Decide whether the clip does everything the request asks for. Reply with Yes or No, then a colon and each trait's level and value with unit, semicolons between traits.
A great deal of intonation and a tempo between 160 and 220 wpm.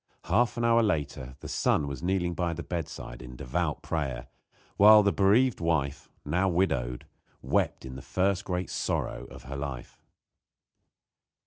No: wide, 6.0 semitones; average, 150 wpm